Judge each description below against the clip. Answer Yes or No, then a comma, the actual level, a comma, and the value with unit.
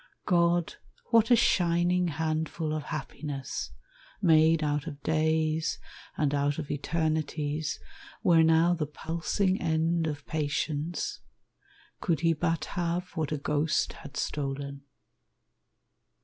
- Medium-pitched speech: Yes, medium, 160 Hz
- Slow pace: Yes, slow, 115 wpm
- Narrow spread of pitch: Yes, narrow, 2.2 semitones